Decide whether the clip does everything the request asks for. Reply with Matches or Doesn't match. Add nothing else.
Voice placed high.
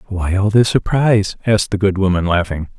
Doesn't match